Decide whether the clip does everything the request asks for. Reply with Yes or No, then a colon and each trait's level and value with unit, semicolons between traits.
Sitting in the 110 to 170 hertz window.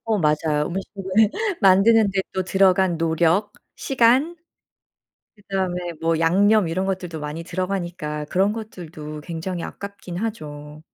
No: medium, 185 Hz